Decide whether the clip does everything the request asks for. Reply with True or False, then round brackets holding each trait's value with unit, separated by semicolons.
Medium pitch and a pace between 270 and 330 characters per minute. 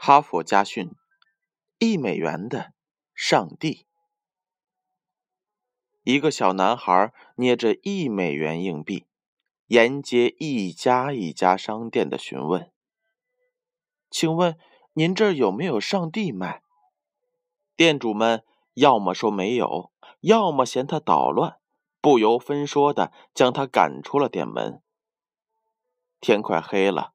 False (165 Hz; 165 characters per minute)